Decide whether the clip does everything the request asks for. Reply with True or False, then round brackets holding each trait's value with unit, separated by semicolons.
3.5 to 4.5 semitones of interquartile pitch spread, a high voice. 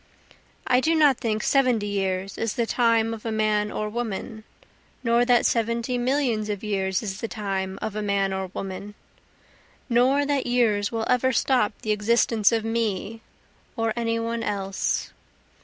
False (2.6 semitones; 225 Hz)